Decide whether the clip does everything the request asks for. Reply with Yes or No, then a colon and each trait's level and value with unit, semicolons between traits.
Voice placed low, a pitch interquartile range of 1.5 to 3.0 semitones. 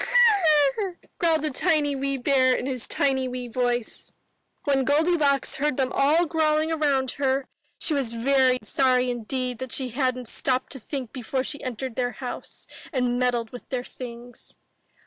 No: very high, 265 Hz; narrow, 2.6 semitones